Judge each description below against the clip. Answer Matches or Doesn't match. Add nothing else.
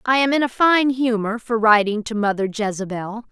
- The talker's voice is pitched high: Matches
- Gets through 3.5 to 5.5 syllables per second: Matches